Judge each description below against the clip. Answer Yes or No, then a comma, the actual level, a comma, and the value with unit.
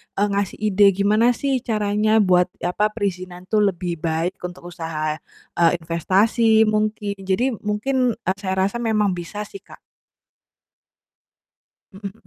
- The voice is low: No, high, 200 Hz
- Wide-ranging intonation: No, average, 3.1 semitones